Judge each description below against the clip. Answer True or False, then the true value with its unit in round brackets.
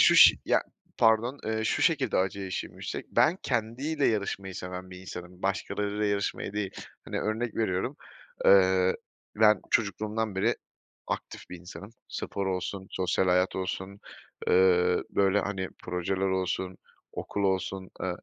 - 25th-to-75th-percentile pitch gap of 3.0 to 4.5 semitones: False (2.5 semitones)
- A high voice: False (95 Hz)